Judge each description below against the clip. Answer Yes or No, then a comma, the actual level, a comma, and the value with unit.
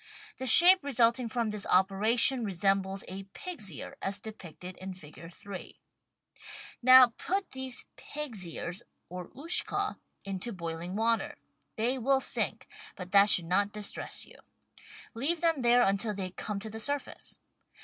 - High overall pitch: Yes, high, 215 Hz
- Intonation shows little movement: No, average, 5.1 semitones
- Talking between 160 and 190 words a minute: No, average, 145 wpm